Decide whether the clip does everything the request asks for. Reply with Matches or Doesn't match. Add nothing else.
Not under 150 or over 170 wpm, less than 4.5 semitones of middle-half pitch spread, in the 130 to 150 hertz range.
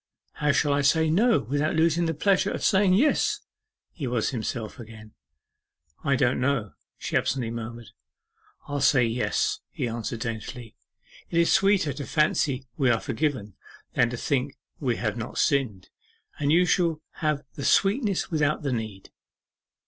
Doesn't match